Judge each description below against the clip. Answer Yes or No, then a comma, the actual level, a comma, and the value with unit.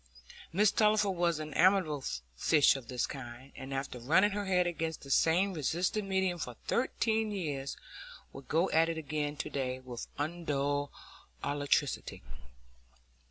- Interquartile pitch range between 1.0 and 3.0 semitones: No, average, 5.3 semitones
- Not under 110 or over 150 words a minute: Yes, average, 145 wpm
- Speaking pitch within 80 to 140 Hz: No, medium, 155 Hz